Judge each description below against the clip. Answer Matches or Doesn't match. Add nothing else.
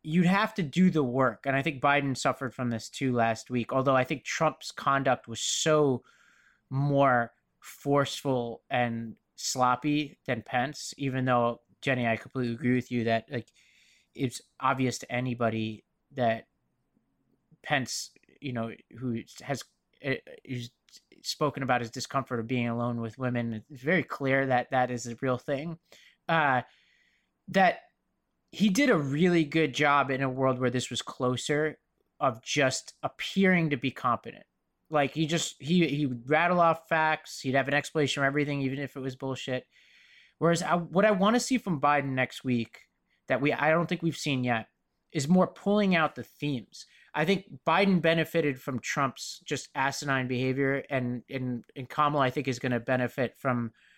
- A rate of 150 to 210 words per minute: Matches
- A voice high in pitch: Doesn't match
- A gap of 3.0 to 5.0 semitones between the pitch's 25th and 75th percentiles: Matches